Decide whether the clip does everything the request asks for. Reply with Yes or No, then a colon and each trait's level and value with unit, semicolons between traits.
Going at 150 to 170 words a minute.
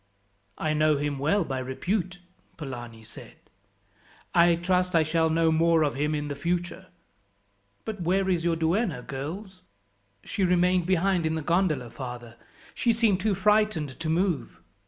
Yes: average, 155 wpm